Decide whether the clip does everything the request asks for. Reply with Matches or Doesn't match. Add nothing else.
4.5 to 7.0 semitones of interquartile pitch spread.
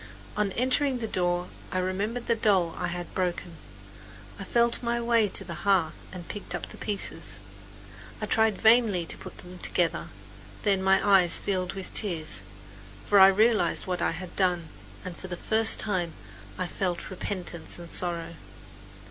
Doesn't match